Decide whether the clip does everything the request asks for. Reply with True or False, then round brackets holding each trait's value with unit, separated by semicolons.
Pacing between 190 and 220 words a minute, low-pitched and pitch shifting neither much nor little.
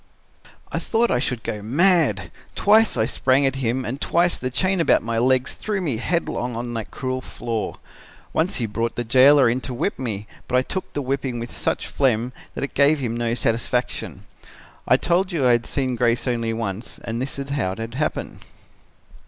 True (195 wpm; 125 Hz; 3.4 semitones)